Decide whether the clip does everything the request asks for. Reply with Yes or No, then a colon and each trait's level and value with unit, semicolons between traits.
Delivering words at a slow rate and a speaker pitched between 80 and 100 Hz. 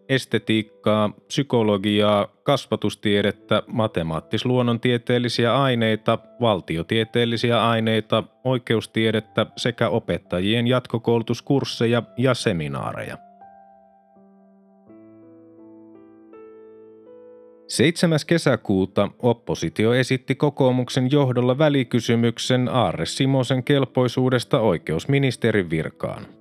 No: slow, 55 wpm; low, 115 Hz